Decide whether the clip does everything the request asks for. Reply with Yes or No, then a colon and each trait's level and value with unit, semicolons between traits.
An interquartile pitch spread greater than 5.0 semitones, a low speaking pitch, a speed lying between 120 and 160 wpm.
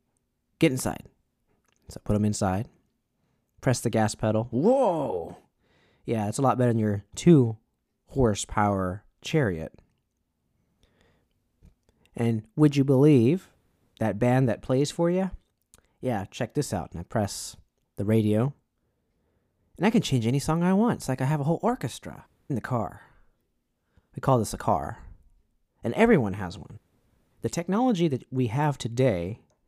Yes: wide, 5.4 semitones; low, 120 Hz; average, 150 wpm